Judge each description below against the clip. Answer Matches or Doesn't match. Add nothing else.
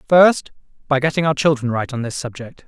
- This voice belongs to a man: Matches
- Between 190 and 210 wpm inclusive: Matches